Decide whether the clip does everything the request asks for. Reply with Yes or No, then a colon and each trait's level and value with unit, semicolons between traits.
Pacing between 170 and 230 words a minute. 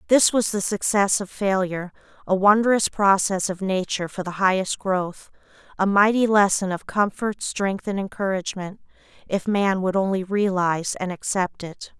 No: average, 150 wpm